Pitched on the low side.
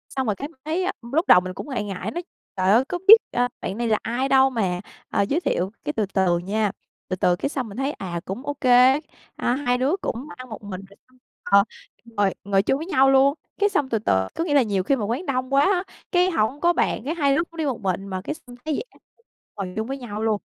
No: high, 245 Hz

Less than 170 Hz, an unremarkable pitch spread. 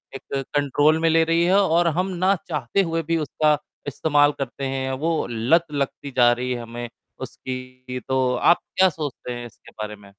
Yes: medium, 140 Hz; average, 4.4 semitones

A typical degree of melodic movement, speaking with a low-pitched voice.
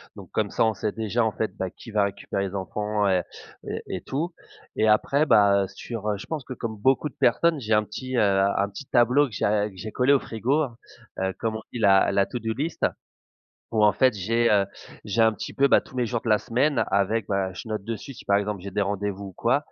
Yes: average, 3.2 semitones; low, 110 Hz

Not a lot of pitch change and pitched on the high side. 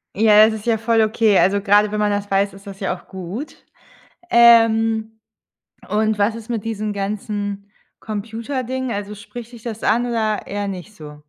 Yes: narrow, 2.0 semitones; high, 215 Hz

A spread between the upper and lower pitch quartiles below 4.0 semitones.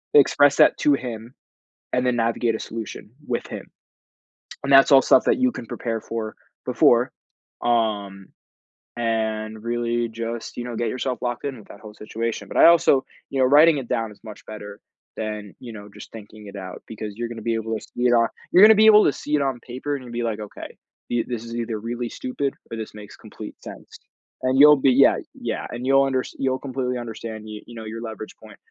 Yes: average, 2.8 semitones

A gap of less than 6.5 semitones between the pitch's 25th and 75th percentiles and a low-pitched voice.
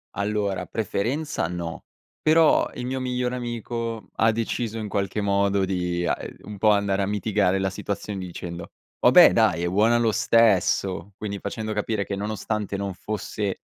Yes: average, 2.7 semitones; low, 105 Hz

